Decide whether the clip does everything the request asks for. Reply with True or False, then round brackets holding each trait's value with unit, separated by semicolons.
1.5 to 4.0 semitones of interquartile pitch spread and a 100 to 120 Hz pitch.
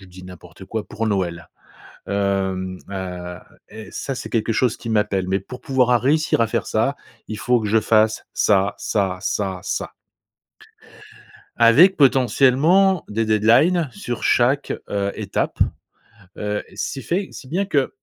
False (5.2 semitones; 110 Hz)